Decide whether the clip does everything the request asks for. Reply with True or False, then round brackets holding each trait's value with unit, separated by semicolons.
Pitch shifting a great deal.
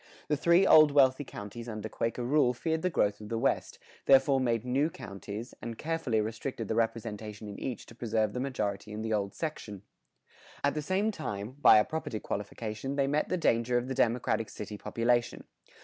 False (4.4 semitones)